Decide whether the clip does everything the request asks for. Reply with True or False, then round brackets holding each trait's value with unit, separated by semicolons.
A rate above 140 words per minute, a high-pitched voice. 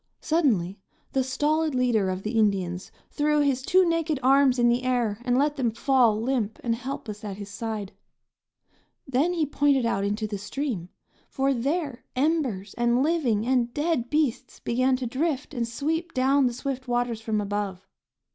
True (165 wpm; 250 Hz)